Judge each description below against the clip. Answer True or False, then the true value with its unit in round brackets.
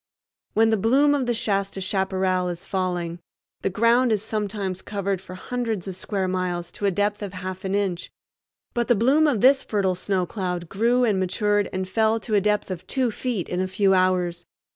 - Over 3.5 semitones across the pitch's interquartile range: False (3.1 semitones)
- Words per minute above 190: True (200 wpm)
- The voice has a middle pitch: False (195 Hz)